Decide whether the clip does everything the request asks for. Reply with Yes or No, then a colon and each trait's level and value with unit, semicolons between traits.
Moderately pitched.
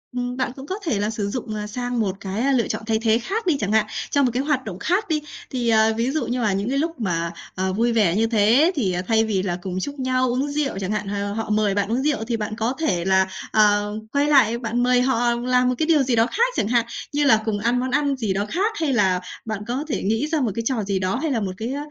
No: high, 230 Hz